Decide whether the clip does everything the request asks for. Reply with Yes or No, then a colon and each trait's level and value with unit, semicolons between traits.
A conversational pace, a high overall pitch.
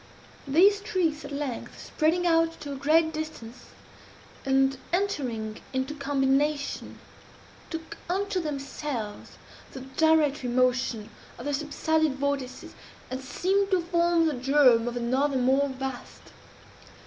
No: slow, 120 wpm; very high, 285 Hz